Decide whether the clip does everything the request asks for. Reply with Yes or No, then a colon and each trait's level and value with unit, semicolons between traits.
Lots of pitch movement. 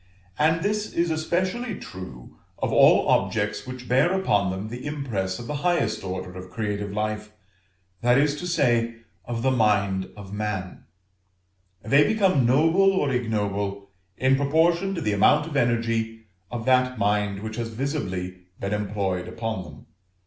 Yes: wide, 6.4 semitones